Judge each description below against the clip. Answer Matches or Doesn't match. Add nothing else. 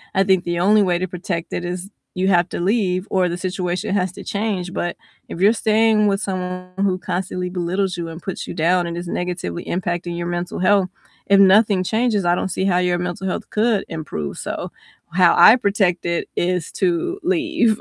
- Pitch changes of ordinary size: Doesn't match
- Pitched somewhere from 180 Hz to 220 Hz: Matches